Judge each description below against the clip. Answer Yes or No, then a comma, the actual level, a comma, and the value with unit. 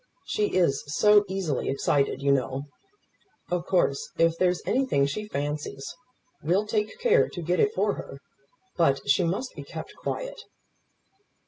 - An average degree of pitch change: No, wide, 7.0 semitones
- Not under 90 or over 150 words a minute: Yes, average, 145 wpm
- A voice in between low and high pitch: Yes, medium, 175 Hz